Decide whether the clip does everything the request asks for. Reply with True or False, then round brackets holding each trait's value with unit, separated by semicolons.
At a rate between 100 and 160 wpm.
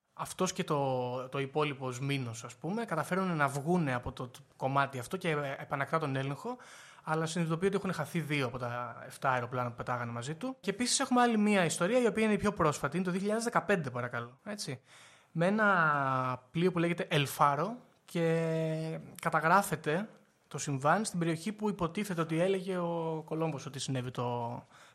False (170 wpm)